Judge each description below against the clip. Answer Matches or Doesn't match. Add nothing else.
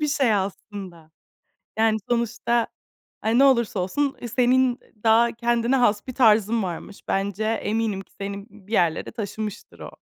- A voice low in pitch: Doesn't match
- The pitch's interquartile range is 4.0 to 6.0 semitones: Doesn't match